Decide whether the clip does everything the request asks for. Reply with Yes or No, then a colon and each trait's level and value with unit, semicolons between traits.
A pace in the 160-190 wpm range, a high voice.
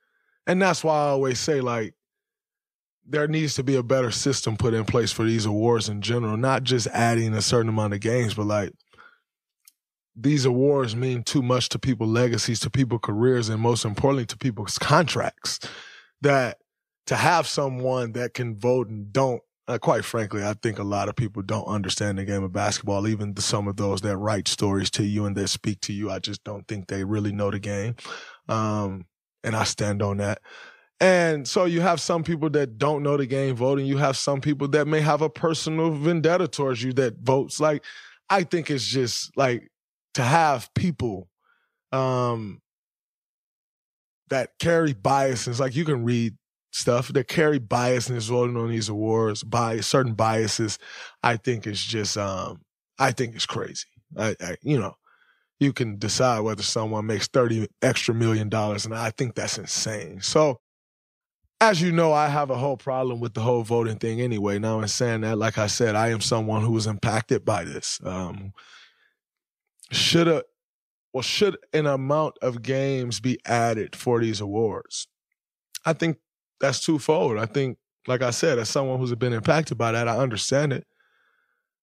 No: average, 185 wpm; low, 120 Hz